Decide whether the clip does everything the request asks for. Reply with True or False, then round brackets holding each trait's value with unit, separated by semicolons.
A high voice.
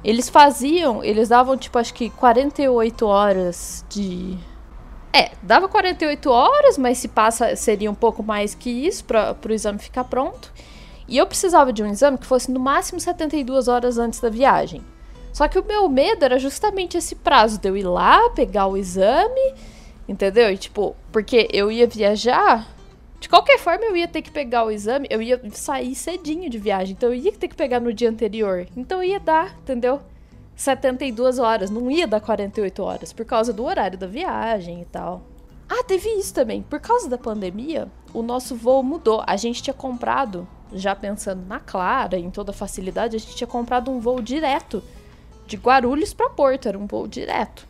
True (245 Hz)